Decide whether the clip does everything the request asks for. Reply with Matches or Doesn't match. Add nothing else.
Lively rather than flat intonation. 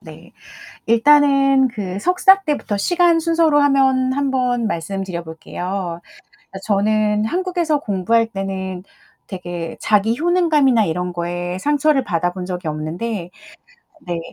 Matches